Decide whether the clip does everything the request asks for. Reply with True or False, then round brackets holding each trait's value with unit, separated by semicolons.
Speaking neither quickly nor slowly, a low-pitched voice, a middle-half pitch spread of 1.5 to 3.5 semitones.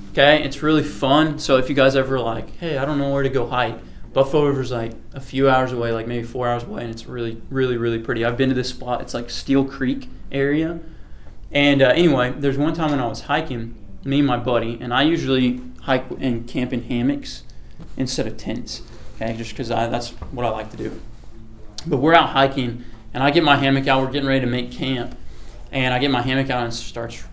False (235 wpm; 130 Hz; 2.9 semitones)